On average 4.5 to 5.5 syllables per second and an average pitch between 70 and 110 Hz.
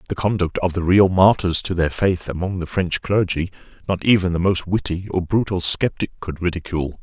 Yes: 5.4 syllables/s; very low, 90 Hz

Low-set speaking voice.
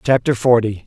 Yes: low, 120 Hz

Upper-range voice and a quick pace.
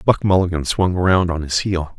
No: very low, 90 Hz; fast, 210 wpm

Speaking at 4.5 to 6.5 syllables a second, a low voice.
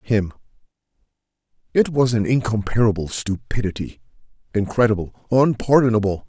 Yes: 5.5 syllables/s; low, 110 Hz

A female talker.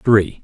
No: male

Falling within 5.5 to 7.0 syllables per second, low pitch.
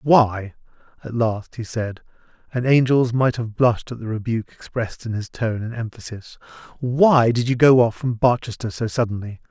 No: 5.1 syllables/s; low, 115 Hz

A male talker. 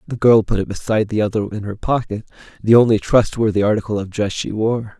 Yes: male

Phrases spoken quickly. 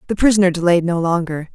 No: average, 195 wpm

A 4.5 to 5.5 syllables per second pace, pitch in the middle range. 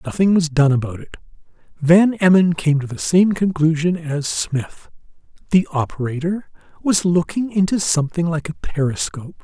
Yes: 4.9 syllables/s; medium, 165 Hz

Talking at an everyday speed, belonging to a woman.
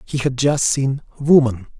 No: average, 165 wpm; male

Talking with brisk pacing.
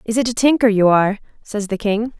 Yes: fast, 245 wpm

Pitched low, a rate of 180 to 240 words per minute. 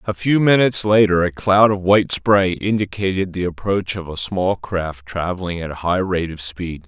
Yes: very low, 95 Hz; average, 200 wpm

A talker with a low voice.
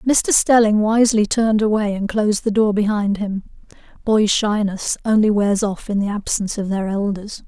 No: high, 210 Hz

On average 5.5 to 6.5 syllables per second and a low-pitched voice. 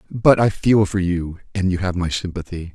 No: 5.0 syllables/s; very low, 95 Hz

